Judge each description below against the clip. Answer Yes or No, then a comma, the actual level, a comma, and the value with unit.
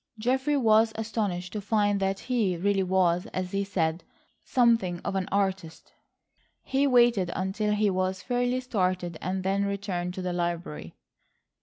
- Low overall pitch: No, high, 195 Hz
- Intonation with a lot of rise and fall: No, average, 3.3 semitones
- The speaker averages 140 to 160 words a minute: Yes, average, 150 wpm